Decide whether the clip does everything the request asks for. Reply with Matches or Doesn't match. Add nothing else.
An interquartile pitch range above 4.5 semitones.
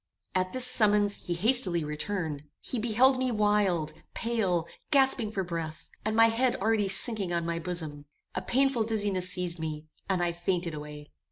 Matches